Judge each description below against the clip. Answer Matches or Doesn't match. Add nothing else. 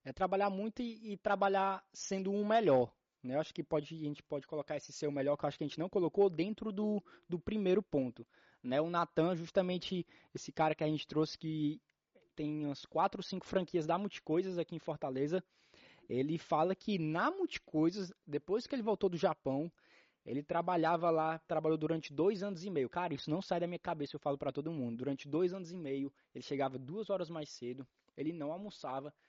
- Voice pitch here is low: Doesn't match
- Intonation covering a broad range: Doesn't match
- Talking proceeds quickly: Matches